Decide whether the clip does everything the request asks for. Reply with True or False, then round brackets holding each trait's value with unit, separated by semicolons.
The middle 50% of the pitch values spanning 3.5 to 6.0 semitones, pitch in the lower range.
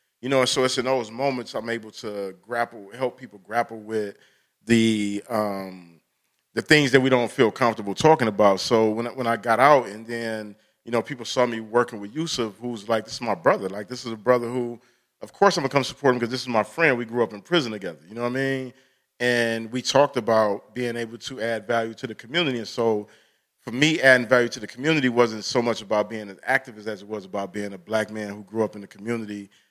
False (2.9 semitones; 115 Hz)